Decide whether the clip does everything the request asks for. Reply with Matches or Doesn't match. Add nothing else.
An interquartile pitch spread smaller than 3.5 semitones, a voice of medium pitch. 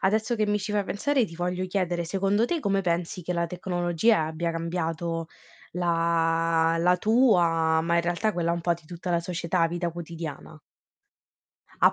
Matches